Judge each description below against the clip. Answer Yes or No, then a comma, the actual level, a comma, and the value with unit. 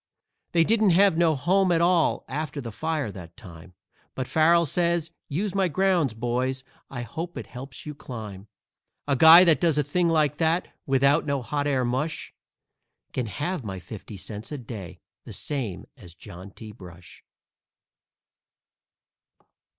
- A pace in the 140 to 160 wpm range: Yes, average, 155 wpm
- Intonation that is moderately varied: No, wide, 6.5 semitones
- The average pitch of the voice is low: No, medium, 145 Hz